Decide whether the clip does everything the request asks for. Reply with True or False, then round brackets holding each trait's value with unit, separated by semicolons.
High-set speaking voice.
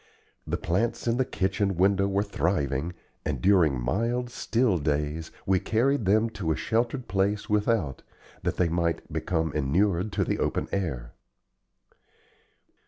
False (95 Hz)